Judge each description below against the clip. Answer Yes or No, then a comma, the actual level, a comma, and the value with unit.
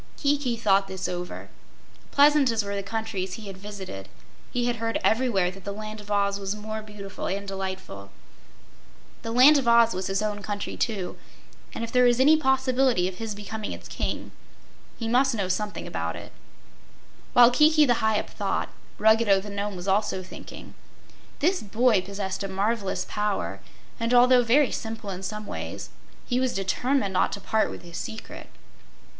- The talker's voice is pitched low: No, high, 215 Hz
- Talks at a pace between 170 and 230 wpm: Yes, average, 175 wpm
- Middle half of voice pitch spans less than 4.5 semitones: Yes, average, 3.7 semitones